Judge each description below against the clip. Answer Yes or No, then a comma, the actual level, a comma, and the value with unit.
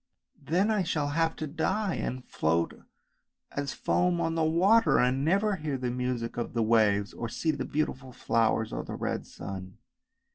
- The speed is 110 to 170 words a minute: No, average, 185 wpm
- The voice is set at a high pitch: No, medium, 140 Hz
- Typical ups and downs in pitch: No, wide, 6.1 semitones